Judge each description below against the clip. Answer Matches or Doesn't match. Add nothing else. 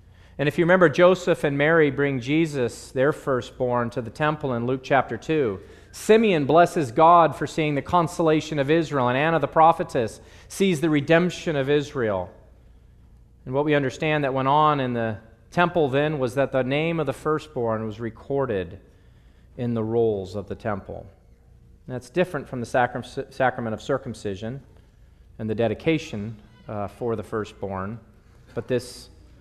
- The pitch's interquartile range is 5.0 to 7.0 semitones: Matches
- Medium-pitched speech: Doesn't match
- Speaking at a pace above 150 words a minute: Matches